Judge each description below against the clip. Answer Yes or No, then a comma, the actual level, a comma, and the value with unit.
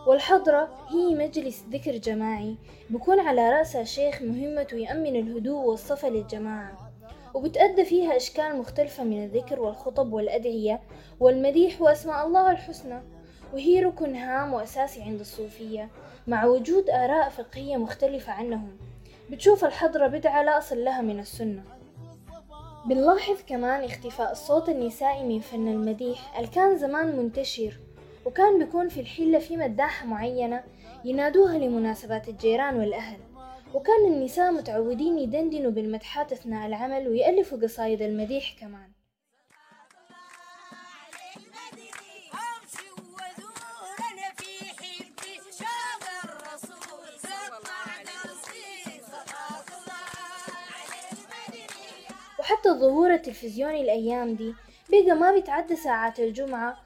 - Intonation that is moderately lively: No, wide, 6.1 semitones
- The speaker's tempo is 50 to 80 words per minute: No, average, 95 wpm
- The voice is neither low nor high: No, very high, 270 Hz